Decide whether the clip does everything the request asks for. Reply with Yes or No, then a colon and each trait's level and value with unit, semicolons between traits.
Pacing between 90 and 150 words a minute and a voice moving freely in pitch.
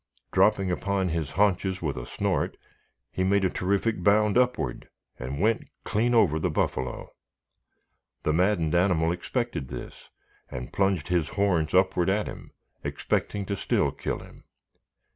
No: average, 145 wpm; average, 3.9 semitones